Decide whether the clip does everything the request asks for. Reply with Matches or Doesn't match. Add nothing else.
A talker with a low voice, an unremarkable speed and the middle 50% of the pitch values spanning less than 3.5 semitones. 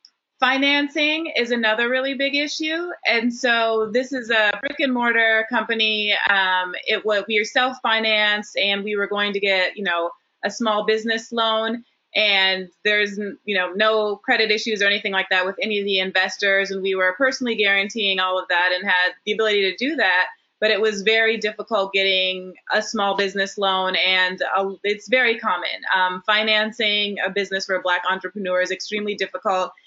Doesn't match